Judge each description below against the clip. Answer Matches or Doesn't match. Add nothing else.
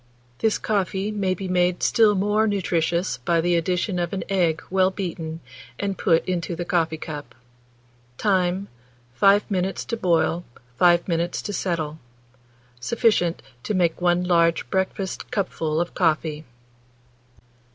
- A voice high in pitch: Doesn't match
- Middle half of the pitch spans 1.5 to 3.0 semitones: Matches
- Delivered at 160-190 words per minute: Doesn't match